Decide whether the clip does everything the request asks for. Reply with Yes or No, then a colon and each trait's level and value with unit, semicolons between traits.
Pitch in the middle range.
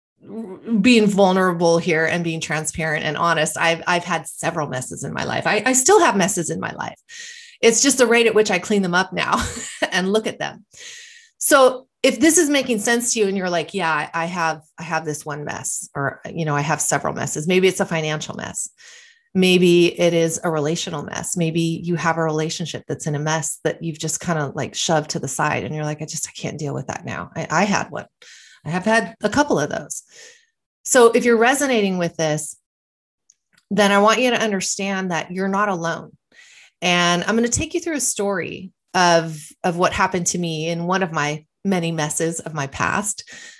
Yes: medium, 180 Hz